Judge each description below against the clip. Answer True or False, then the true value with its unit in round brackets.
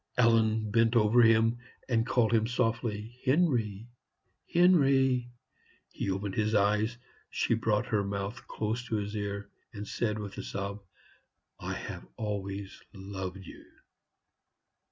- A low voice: True (110 Hz)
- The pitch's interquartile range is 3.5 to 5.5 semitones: False (2.8 semitones)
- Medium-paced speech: False (130 wpm)